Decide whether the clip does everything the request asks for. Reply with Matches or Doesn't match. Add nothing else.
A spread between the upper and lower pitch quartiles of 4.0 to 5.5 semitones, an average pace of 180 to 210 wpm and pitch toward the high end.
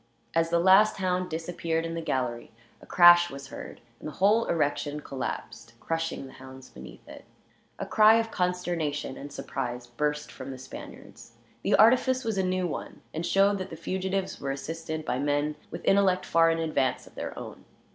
Doesn't match